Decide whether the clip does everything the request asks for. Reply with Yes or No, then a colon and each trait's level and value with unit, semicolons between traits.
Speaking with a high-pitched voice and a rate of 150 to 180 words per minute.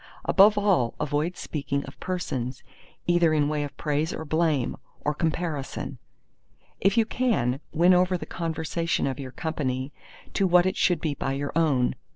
No: medium, 155 Hz; average, 165 wpm